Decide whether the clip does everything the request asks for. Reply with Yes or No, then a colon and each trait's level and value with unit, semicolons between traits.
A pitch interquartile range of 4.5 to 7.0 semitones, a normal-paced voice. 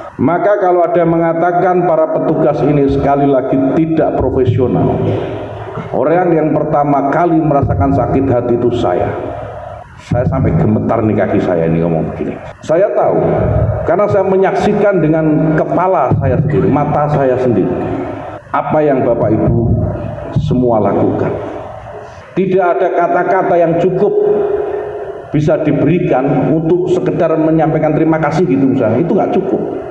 Yes: average, 5.0 semitones; average, 130 wpm